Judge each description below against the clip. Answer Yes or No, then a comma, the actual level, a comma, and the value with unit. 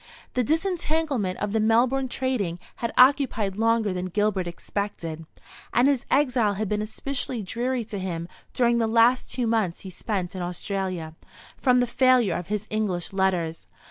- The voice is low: No, high, 215 Hz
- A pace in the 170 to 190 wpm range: No, average, 160 wpm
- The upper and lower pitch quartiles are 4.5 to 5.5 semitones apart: Yes, average, 4.9 semitones